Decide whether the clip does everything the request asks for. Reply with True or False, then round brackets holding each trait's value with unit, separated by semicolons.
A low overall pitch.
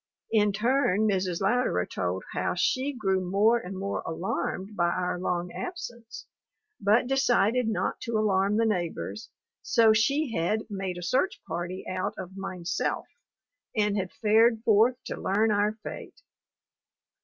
False (205 Hz)